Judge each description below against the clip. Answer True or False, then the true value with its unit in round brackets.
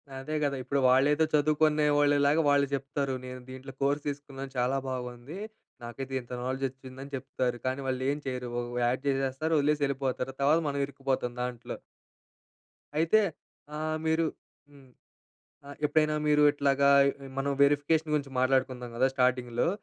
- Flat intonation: True (2.1 semitones)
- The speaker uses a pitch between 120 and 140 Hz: True (135 Hz)